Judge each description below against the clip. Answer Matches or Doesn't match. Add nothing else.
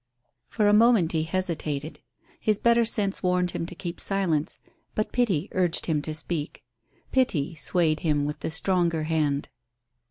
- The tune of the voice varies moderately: Matches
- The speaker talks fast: Doesn't match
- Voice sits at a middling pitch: Matches